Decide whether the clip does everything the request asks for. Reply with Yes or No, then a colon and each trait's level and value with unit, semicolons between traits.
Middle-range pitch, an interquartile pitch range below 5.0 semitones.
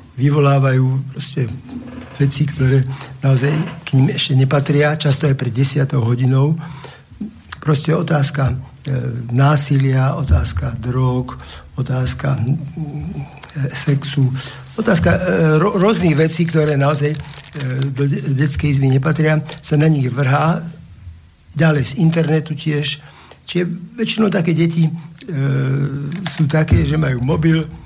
Yes: medium, 145 Hz; average, 2.9 semitones